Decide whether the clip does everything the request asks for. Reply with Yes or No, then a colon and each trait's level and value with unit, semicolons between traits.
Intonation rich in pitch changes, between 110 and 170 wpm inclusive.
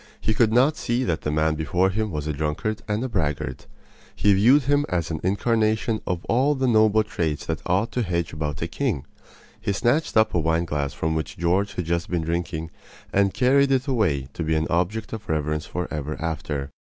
No: wide, 5.9 semitones; fast, 205 wpm